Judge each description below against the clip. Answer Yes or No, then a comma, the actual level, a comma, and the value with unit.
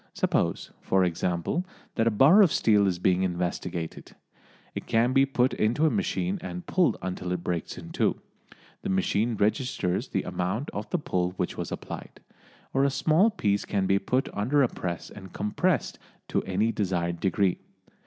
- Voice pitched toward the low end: Yes, low, 100 Hz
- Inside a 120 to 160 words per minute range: No, average, 175 wpm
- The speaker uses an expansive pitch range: Yes, wide, 6.7 semitones